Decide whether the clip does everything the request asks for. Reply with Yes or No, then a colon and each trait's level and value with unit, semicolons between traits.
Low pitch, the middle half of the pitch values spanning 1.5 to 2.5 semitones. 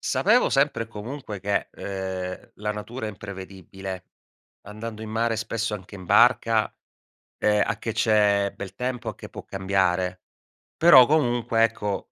No: low, 105 Hz; average, 2.9 semitones